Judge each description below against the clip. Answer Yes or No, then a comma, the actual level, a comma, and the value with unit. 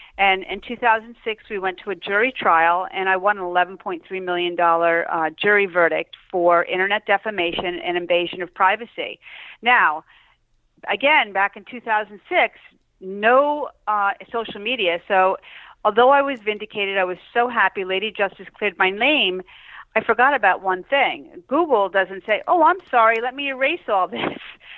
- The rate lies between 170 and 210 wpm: No, average, 155 wpm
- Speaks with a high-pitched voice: Yes, high, 200 Hz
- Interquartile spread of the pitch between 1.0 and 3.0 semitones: No, average, 4.3 semitones